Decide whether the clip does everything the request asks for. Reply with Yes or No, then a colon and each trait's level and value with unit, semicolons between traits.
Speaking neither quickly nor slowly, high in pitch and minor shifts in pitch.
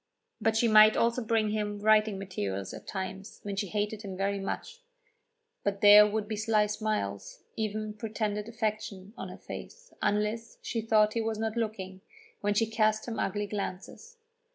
Yes: average, 170 wpm; high, 215 Hz; narrow, 1.4 semitones